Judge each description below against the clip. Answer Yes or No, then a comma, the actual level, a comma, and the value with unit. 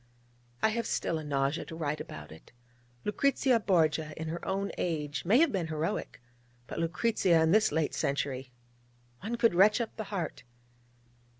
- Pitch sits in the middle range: Yes, medium, 170 Hz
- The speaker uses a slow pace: No, average, 165 wpm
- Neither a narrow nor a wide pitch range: No, wide, 5.7 semitones